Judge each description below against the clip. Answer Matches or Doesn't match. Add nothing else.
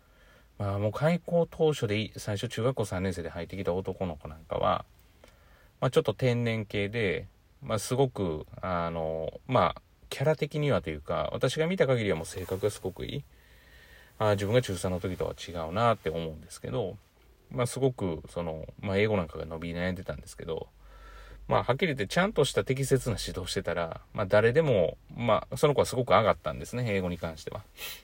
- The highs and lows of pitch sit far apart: Matches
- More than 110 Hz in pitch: Doesn't match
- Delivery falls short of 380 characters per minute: Matches